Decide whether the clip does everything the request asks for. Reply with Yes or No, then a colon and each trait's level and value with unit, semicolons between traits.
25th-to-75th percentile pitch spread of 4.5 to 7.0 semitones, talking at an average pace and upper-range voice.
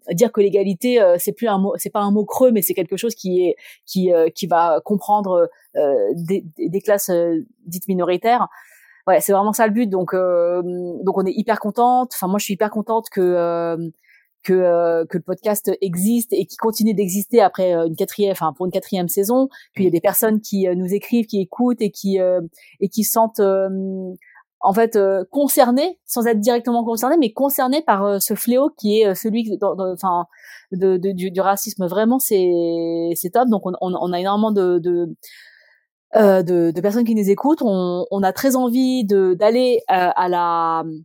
No: average, 3.8 semitones; average, 210 wpm; high, 200 Hz